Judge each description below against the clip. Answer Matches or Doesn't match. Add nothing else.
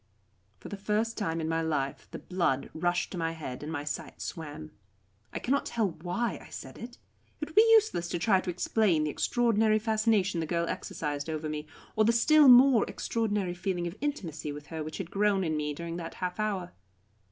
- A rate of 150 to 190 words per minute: Doesn't match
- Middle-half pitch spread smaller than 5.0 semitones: Doesn't match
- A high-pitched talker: Doesn't match